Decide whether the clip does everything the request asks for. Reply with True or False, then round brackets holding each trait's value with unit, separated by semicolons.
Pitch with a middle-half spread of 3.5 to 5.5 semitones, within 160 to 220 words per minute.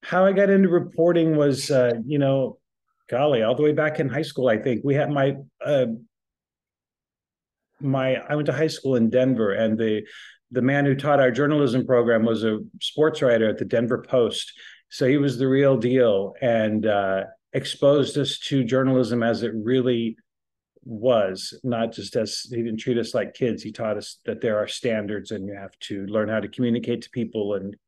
True (4.2 semitones; 195 wpm)